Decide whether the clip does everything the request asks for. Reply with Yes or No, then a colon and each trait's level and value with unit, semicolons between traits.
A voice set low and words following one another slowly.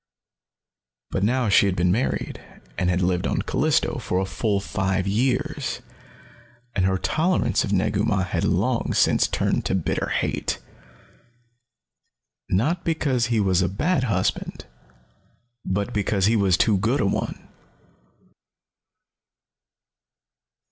Yes: low, 100 Hz; slow, 125 wpm